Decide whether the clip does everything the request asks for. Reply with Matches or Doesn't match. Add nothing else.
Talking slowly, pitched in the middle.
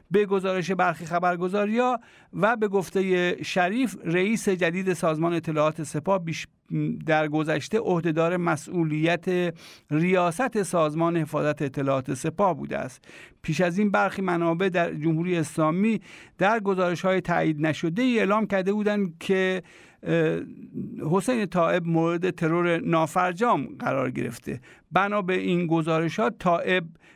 Matches